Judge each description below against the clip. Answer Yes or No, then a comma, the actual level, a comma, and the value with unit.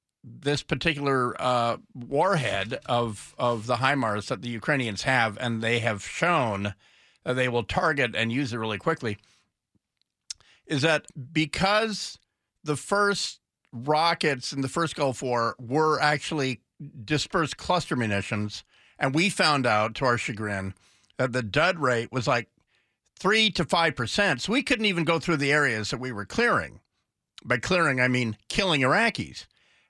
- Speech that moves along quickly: No, average, 150 wpm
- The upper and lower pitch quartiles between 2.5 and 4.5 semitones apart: No, average, 5.2 semitones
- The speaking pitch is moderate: No, low, 130 Hz